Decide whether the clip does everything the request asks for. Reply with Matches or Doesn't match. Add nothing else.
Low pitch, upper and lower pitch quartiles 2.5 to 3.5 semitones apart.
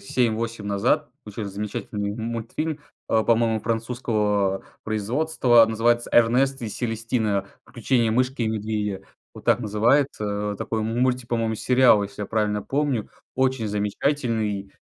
Matches